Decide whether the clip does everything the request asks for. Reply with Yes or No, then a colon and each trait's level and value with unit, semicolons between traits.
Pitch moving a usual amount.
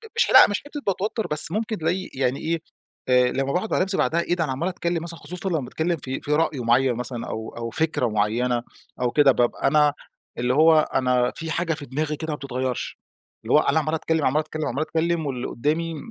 Yes: average, 4.6 semitones